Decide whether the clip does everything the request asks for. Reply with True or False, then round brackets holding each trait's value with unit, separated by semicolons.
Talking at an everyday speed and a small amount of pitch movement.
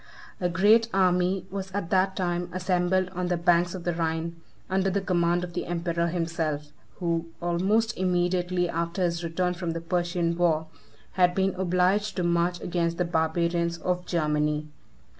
True (160 wpm; 1.4 semitones)